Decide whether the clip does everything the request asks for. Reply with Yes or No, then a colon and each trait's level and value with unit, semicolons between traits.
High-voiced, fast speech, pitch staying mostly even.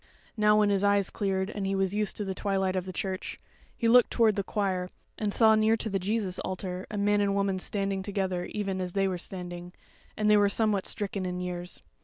Yes: high, 195 Hz; fast, 230 wpm; narrow, 1.8 semitones